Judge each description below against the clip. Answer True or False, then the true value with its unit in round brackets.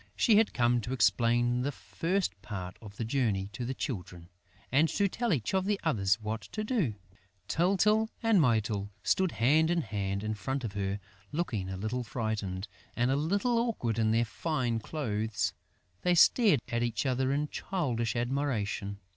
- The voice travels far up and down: True (7.1 semitones)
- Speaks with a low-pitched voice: True (120 Hz)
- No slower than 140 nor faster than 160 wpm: False (170 wpm)